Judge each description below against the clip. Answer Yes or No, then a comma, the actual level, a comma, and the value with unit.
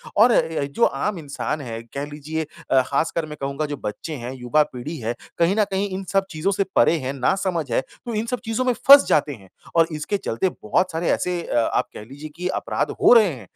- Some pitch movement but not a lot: No, wide, 5.7 semitones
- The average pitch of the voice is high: No, medium, 155 Hz